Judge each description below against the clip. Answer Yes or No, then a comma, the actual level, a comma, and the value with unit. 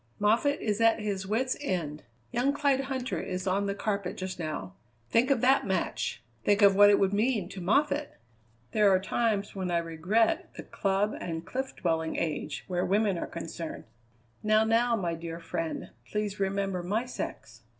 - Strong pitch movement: No, average, 4.2 semitones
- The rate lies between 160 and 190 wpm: Yes, average, 175 wpm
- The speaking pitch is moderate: No, high, 200 Hz